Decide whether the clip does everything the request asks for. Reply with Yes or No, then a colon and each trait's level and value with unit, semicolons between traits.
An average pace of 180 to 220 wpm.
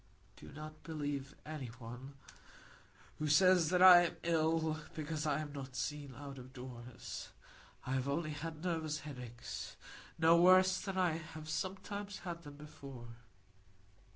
No: slow, 135 wpm